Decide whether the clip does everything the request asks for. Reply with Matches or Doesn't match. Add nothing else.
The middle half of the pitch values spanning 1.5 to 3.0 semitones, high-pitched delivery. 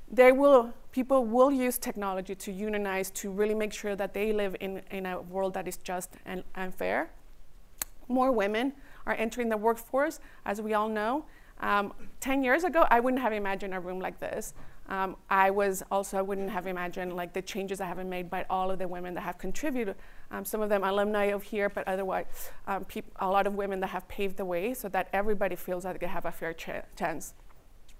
Matches